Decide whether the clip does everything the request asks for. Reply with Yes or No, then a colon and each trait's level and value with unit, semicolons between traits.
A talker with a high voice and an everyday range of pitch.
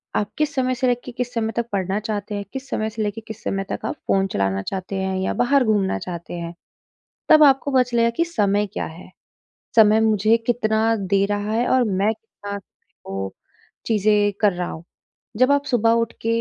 Yes: high, 215 Hz; average, 3.6 semitones